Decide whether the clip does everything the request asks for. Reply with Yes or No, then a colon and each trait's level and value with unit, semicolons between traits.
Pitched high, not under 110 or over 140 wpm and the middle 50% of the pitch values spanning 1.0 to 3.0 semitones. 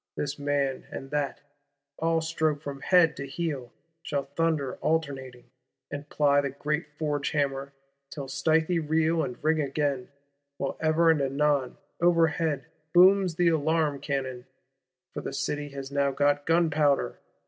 No: medium, 145 Hz; slow, 135 wpm; narrow, 2.6 semitones